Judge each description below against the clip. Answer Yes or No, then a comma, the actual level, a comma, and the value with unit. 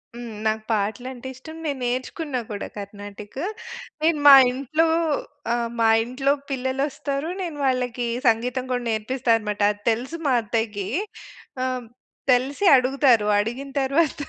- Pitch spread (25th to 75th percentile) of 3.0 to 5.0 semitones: Yes, average, 3.5 semitones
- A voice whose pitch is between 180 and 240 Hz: No, very high, 250 Hz